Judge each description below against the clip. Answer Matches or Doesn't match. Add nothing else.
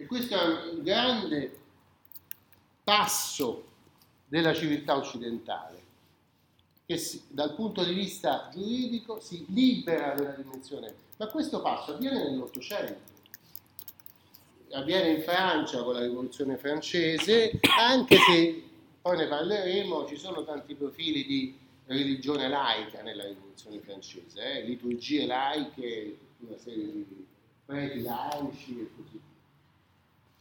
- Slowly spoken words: Matches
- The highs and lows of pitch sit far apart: Matches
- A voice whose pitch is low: Doesn't match